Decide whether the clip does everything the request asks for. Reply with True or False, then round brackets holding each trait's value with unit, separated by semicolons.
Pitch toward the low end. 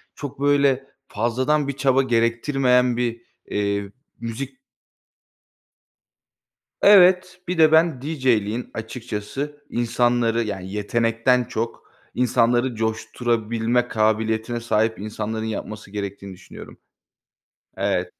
True (115 Hz)